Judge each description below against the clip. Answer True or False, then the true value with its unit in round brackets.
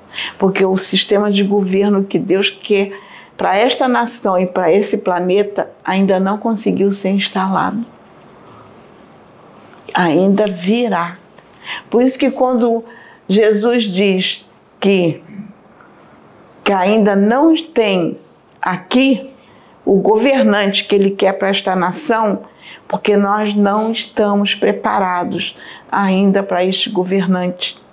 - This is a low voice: False (200 Hz)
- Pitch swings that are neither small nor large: False (2.3 semitones)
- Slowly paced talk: True (110 wpm)